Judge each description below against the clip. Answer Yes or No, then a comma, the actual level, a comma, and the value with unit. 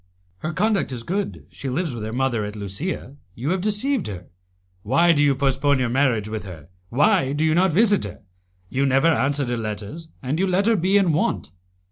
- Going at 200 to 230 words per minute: Yes, fast, 205 wpm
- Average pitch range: No, wide, 7.3 semitones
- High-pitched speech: No, medium, 140 Hz